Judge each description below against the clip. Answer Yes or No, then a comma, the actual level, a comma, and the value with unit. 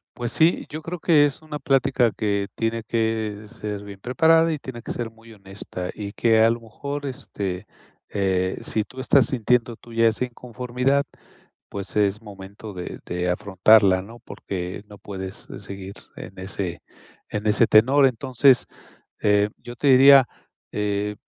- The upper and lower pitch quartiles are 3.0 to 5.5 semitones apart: Yes, average, 4.1 semitones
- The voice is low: Yes, low, 110 Hz